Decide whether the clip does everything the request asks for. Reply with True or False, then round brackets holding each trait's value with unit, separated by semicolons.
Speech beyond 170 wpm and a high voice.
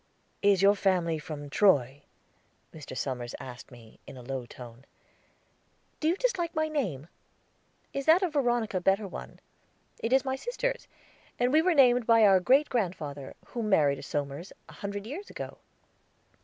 False (165 wpm; 200 Hz)